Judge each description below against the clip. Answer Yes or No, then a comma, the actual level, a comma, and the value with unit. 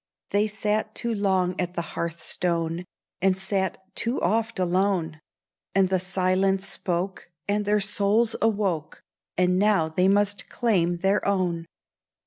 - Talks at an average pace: No, slow, 130 wpm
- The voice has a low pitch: No, high, 190 Hz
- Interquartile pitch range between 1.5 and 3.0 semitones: Yes, narrow, 2.5 semitones